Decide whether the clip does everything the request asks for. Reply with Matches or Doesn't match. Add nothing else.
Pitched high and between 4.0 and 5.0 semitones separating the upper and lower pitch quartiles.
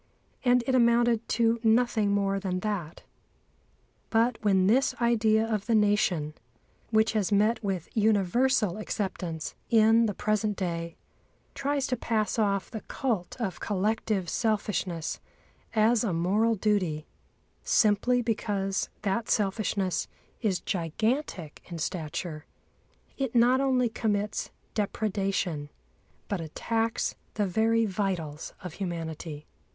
Doesn't match